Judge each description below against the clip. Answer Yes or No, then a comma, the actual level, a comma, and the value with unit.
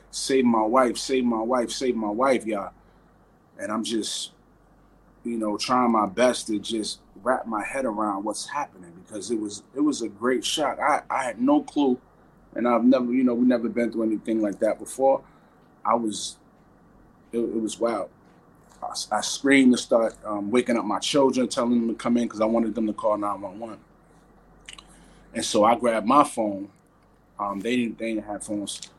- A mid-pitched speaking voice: No, low, 115 Hz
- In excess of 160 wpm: Yes, average, 195 wpm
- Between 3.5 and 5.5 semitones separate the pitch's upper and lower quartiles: No, average, 2.9 semitones